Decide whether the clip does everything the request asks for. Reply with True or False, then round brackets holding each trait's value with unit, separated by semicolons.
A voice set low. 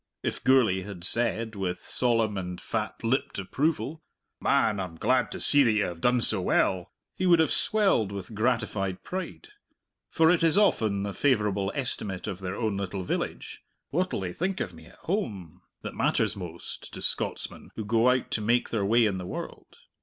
True (110 Hz)